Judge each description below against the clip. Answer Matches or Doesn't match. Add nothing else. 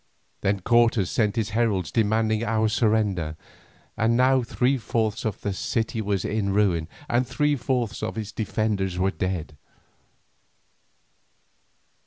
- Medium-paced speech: Doesn't match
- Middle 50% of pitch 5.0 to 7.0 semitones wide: Doesn't match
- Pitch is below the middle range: Matches